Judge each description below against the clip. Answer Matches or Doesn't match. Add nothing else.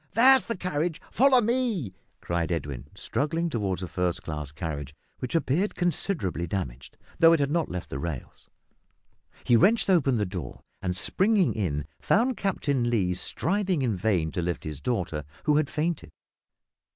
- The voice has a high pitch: Doesn't match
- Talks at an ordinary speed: Matches